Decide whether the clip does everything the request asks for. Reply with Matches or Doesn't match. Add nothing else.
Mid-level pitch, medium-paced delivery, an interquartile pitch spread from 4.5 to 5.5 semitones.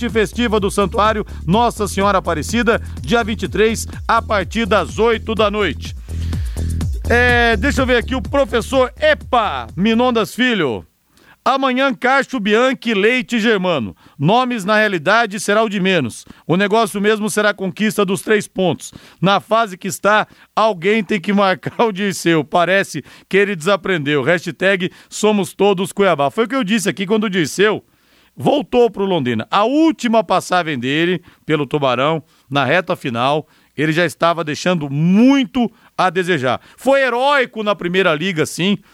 Doesn't match